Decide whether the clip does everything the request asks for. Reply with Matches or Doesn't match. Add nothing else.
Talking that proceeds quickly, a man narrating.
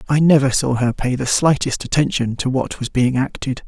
Matches